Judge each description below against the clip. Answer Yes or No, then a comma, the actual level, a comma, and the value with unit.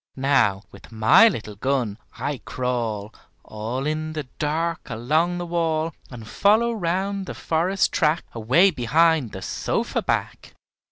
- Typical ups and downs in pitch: No, wide, 6.3 semitones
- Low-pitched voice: No, medium, 150 Hz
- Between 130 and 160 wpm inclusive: Yes, slow, 135 wpm